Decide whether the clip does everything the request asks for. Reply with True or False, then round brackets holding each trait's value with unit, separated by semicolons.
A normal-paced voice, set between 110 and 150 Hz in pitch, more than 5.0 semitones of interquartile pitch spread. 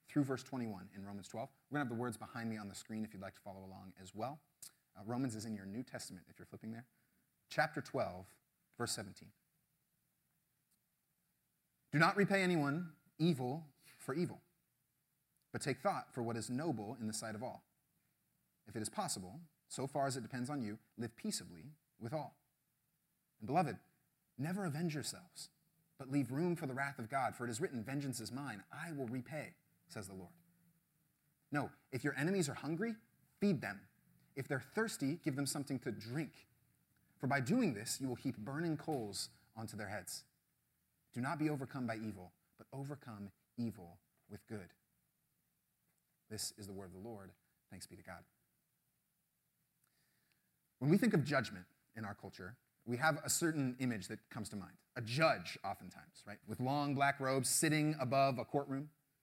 True (180 wpm; 135 Hz; 5.5 semitones)